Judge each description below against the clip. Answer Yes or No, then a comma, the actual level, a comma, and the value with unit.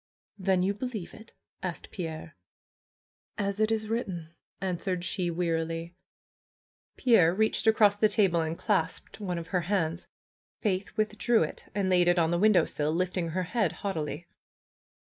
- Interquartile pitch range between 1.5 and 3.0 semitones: No, average, 3.7 semitones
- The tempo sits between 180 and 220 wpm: No, average, 150 wpm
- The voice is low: No, medium, 185 Hz